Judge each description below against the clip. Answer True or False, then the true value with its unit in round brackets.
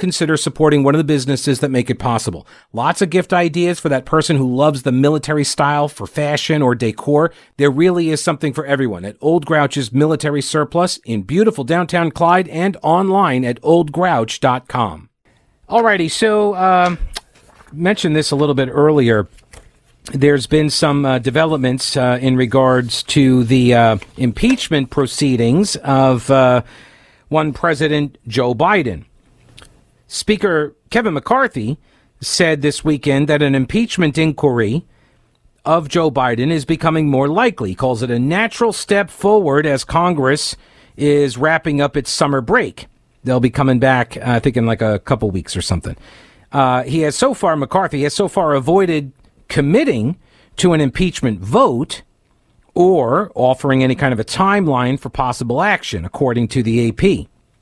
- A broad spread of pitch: False (4.3 semitones)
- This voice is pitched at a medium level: True (145 Hz)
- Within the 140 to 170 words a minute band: True (155 wpm)